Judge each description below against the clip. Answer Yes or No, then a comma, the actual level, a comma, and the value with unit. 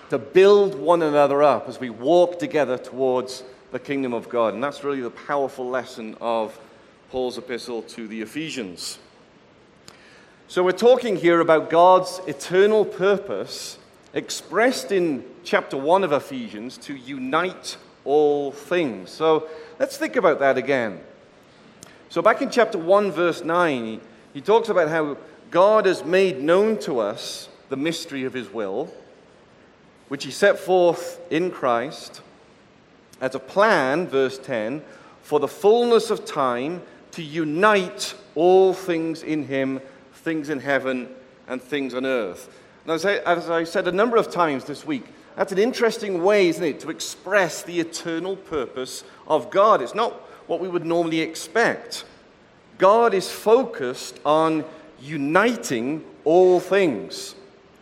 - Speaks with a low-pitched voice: No, medium, 165 Hz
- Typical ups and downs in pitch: No, wide, 6.3 semitones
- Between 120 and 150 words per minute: Yes, average, 145 wpm